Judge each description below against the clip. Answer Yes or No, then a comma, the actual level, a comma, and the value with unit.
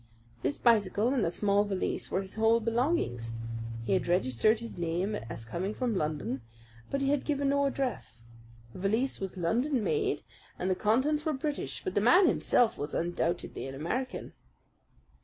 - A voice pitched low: No, high, 215 Hz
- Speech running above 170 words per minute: No, average, 165 wpm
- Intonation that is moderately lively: No, wide, 7.5 semitones